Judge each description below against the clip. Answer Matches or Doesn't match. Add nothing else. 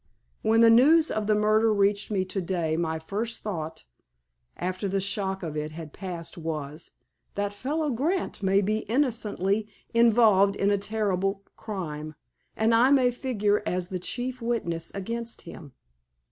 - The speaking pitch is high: Matches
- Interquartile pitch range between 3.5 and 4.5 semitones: Matches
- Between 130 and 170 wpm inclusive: Matches